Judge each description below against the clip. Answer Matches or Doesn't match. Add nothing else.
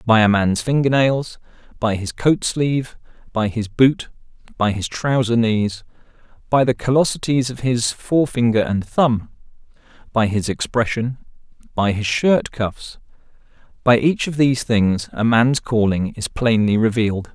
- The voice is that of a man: Matches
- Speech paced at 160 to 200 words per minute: Doesn't match